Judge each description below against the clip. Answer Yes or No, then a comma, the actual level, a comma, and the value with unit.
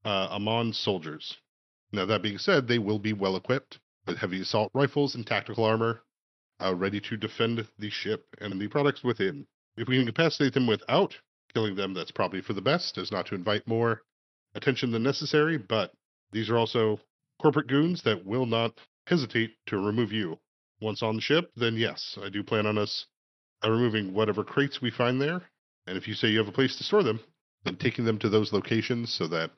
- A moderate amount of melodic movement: Yes, average, 3.3 semitones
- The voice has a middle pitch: No, low, 115 Hz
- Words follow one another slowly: No, fast, 205 wpm